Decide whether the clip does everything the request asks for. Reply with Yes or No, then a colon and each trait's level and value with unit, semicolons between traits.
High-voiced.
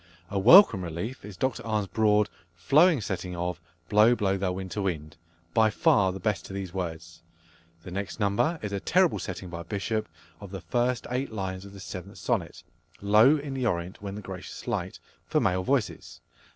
No: low, 100 Hz